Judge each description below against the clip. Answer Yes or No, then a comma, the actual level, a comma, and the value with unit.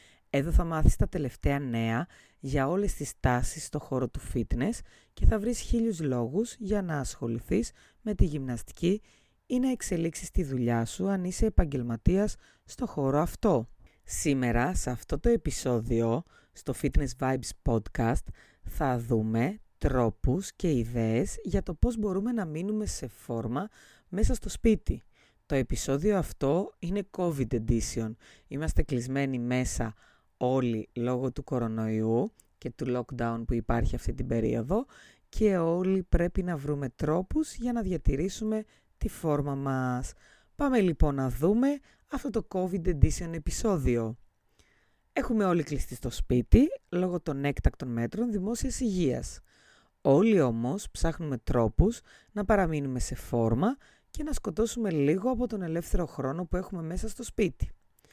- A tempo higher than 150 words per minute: No, average, 140 wpm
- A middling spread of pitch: No, wide, 8.4 semitones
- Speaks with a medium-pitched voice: Yes, medium, 145 Hz